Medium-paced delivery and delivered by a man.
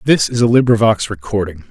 Yes: average, 175 wpm; male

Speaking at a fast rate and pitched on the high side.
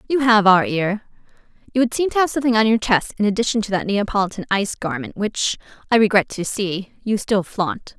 Yes: fast, 210 wpm; high, 210 Hz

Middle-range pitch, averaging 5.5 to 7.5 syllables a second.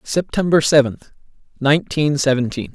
No: medium, 145 Hz; 5.1 syllables/s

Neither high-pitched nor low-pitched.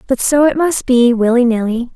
No: very high, 250 Hz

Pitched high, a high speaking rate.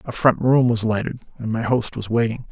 No: low, 115 Hz; fast, 215 wpm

